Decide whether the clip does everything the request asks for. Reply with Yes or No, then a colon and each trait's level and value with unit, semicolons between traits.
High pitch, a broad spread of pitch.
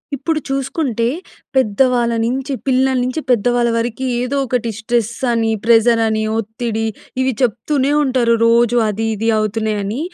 No: high, 235 Hz; narrow, 2.6 semitones